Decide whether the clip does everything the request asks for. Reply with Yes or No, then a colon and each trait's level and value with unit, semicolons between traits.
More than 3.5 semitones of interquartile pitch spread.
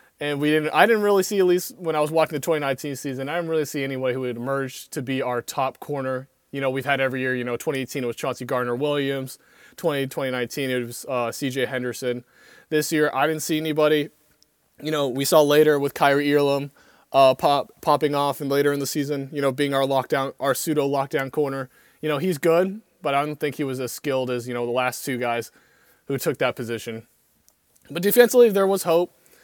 No: average, 2.7 semitones